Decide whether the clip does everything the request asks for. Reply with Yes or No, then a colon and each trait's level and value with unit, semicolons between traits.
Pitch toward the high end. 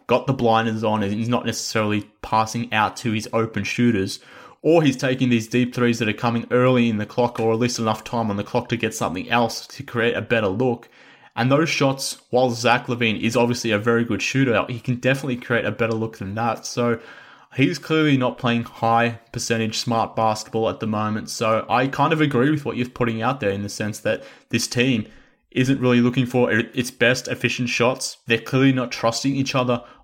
No: low, 120 Hz